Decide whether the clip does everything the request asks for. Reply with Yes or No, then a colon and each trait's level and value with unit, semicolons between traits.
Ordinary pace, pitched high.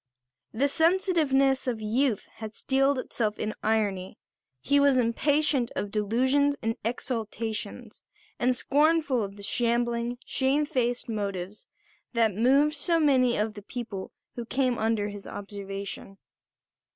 No: slow, 125 wpm; high, 240 Hz